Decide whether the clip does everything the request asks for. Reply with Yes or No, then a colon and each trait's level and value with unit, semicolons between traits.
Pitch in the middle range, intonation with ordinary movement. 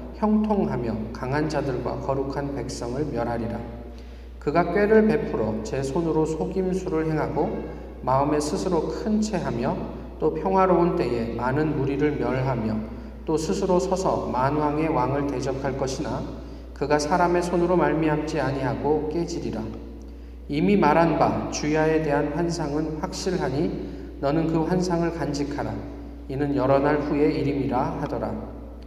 Yes: medium, 150 Hz; average, 4.3 semitones